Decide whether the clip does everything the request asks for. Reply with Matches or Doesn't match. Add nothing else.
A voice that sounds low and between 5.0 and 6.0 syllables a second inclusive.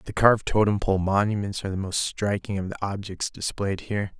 Matches